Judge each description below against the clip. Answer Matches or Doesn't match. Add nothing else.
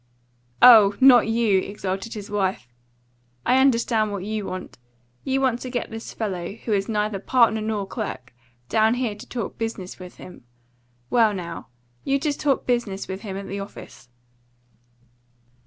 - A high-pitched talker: Matches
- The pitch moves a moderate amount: Matches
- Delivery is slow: Doesn't match